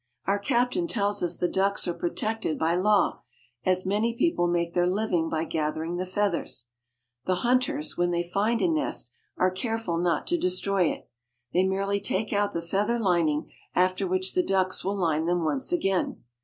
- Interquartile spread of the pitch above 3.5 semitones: No, average, 3.1 semitones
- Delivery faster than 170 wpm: Yes, average, 185 wpm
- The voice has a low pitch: No, medium, 185 Hz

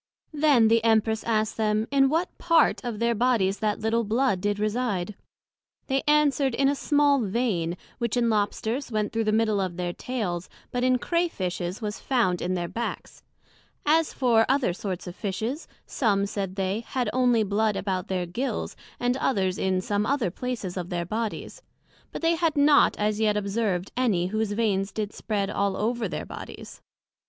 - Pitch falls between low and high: No, high, 220 Hz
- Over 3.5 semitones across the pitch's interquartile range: Yes, average, 4.3 semitones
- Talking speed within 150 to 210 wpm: Yes, average, 180 wpm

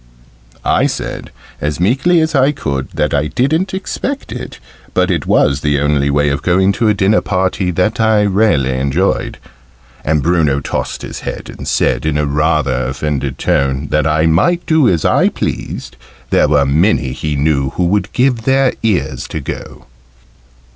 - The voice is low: Yes, very low, 80 Hz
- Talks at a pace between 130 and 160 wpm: No, average, 170 wpm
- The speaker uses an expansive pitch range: Yes, wide, 7.4 semitones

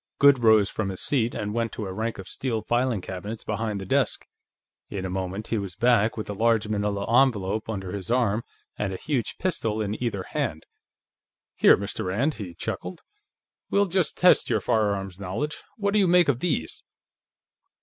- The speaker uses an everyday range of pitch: Yes, average, 3.8 semitones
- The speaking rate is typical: Yes, average, 185 wpm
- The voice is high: No, low, 110 Hz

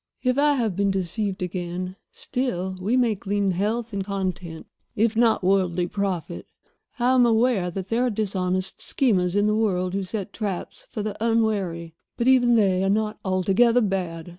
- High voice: Yes, high, 200 Hz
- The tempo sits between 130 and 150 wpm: No, average, 170 wpm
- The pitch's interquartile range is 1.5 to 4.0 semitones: Yes, average, 3.6 semitones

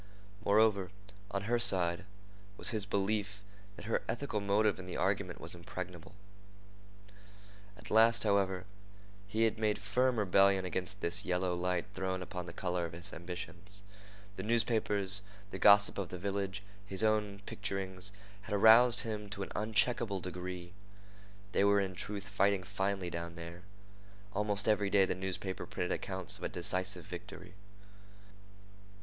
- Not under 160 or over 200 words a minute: No, average, 145 wpm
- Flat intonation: Yes, narrow, 2.3 semitones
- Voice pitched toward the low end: Yes, low, 100 Hz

